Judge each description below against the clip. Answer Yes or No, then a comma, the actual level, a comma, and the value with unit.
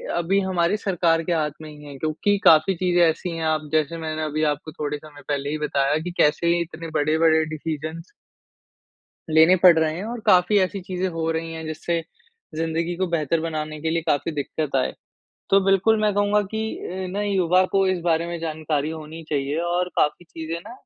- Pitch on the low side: No, medium, 165 Hz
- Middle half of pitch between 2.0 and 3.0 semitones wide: Yes, average, 2.7 semitones